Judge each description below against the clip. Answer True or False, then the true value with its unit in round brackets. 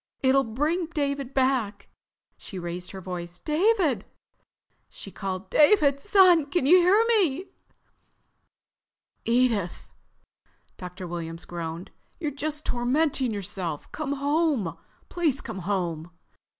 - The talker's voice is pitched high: True (260 Hz)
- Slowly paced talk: True (110 wpm)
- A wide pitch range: True (8.7 semitones)